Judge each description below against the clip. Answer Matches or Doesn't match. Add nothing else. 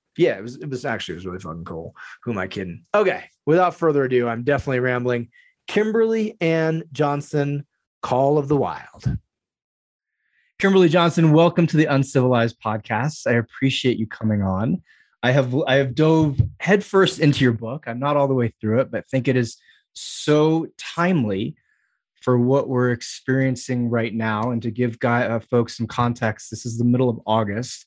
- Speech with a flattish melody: Doesn't match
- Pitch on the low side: Matches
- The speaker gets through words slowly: Doesn't match